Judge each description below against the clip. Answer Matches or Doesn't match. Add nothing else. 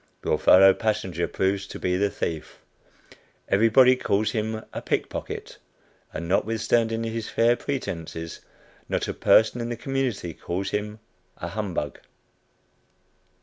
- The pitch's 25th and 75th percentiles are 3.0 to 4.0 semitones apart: Matches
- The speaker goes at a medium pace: Doesn't match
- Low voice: Matches